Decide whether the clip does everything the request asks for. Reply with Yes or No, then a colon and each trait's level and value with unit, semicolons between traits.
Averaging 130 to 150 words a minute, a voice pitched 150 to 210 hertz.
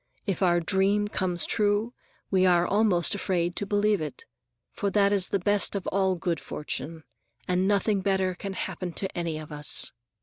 No: average, 175 wpm; high, 190 Hz